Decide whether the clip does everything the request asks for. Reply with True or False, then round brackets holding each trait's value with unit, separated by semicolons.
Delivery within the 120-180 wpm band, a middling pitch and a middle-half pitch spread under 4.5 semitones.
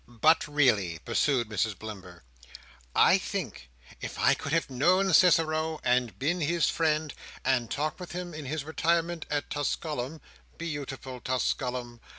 False (150 wpm; 145 Hz; 4.9 semitones)